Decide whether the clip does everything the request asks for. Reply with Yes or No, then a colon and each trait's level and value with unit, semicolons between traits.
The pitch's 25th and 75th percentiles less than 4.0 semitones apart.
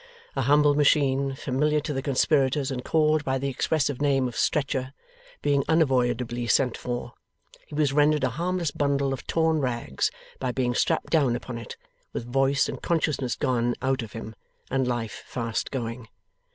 Yes: average, 2.9 semitones